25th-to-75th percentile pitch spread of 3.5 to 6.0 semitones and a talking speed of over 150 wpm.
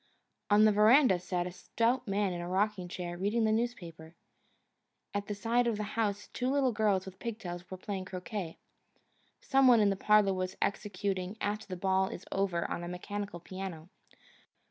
No: average, 2.8 semitones; average, 185 wpm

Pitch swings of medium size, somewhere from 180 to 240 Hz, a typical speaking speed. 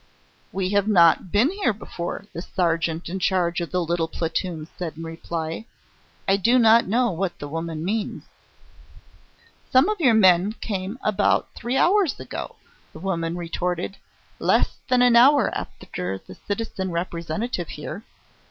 Yes: average, 4.8 semitones; medium, 185 Hz; average, 150 wpm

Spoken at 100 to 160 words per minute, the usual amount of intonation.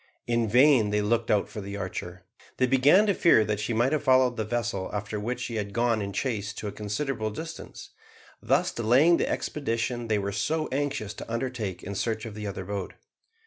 No: fast, 205 wpm; average, 3.8 semitones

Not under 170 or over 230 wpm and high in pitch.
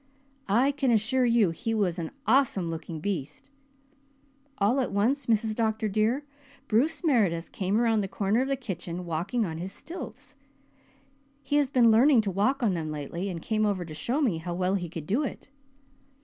Yes: average, 185 wpm; high, 215 Hz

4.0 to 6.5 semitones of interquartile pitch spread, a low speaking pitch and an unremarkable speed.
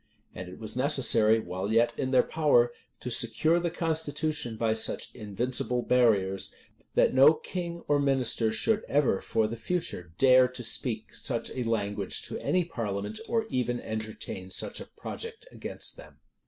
Yes: average, 4.9 semitones; low, 120 Hz; average, 160 wpm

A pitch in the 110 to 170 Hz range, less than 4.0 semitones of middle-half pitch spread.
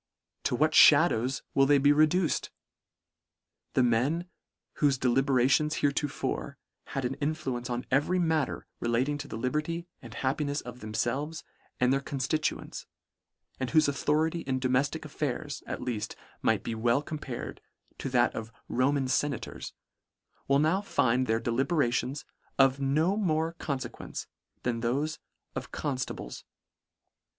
Yes: low, 135 Hz; average, 3.4 semitones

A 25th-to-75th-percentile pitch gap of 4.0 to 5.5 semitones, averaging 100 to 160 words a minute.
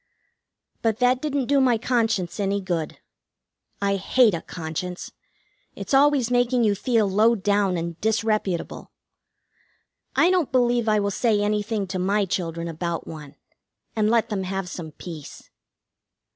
Yes: average, 4.6 semitones; average, 145 wpm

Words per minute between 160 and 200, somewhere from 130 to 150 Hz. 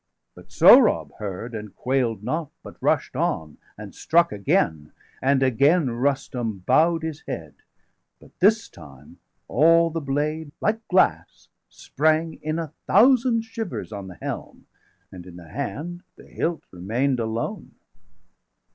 No: average, 140 wpm; medium, 140 Hz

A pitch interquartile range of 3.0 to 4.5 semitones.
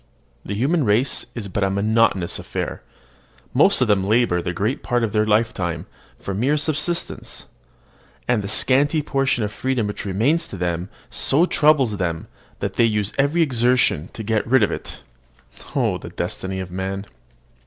No: average, 5.2 semitones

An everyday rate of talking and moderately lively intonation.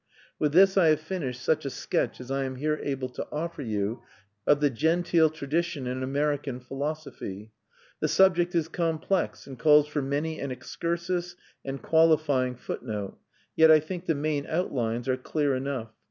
Yes: average, 170 wpm; average, 3.8 semitones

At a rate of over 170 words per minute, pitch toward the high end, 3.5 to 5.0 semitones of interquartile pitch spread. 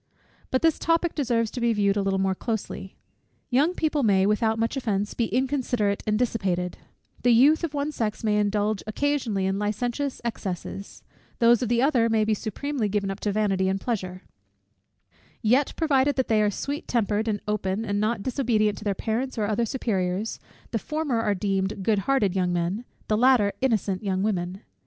Yes: average, 185 wpm; high, 215 Hz; average, 3.9 semitones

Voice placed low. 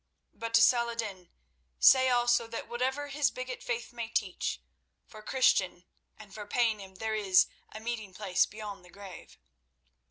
No: high, 225 Hz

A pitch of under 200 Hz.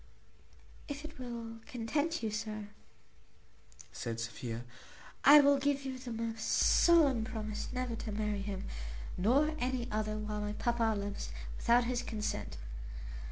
No: high, 225 Hz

